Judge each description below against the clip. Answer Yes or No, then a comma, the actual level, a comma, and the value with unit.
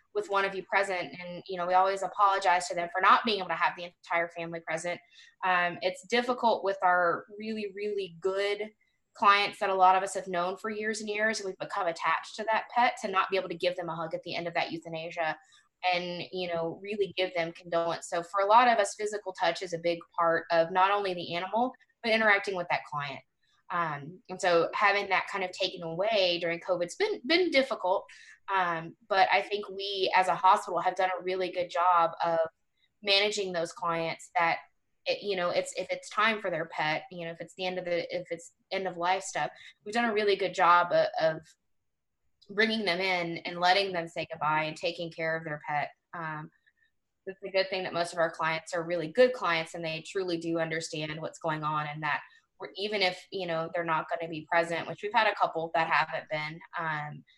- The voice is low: No, medium, 180 Hz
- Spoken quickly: Yes, fast, 225 wpm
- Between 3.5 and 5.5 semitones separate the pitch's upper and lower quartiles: No, average, 3.1 semitones